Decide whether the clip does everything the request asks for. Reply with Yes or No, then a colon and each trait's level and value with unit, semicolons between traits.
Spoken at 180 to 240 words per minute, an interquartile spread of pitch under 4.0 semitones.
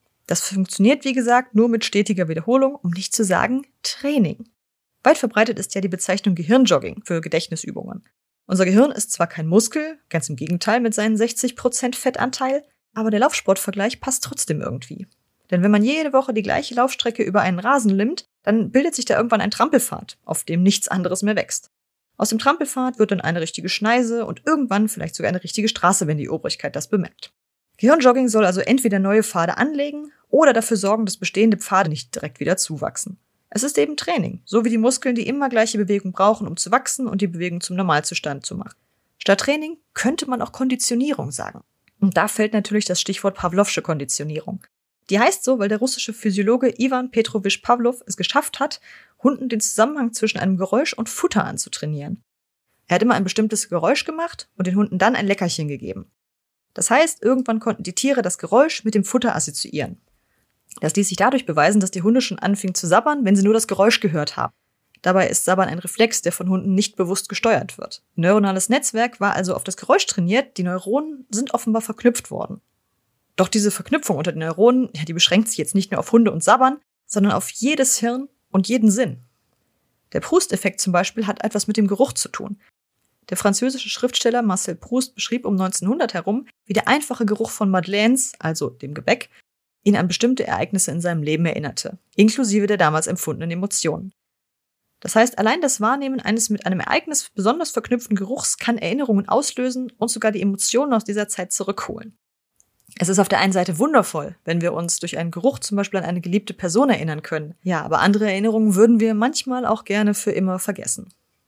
No: fast, 190 wpm; average, 4.8 semitones